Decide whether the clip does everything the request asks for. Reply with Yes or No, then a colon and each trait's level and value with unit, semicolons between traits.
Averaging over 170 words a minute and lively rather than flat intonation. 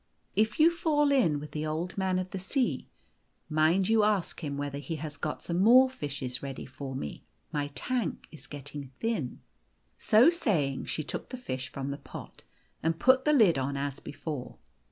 Yes: average, 190 wpm; wide, 7.6 semitones